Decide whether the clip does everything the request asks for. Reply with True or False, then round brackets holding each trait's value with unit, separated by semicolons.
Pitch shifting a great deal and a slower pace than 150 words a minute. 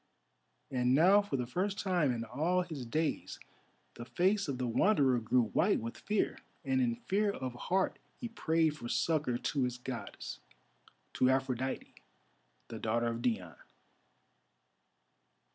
True (6.5 semitones; 140 wpm)